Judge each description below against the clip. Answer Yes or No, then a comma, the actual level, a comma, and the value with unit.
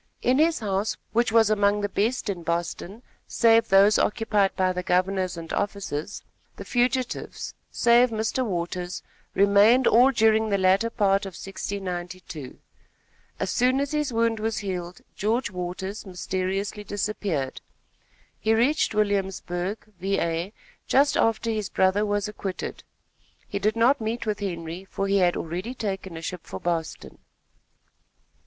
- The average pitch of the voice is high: Yes, high, 200 Hz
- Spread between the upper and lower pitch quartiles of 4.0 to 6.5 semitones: No, average, 3.4 semitones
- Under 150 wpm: Yes, average, 140 wpm